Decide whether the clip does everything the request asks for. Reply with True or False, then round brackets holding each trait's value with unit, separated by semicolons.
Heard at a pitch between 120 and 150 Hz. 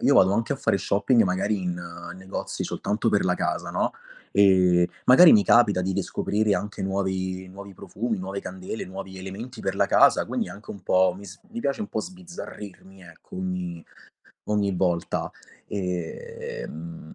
False (95 Hz)